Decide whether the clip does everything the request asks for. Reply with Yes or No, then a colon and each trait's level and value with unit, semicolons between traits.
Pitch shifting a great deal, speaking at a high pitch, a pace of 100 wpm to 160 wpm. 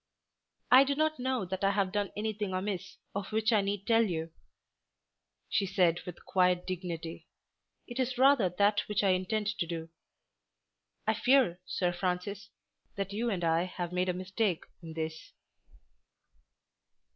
No: average, 3.2 semitones; high, 195 Hz; average, 155 wpm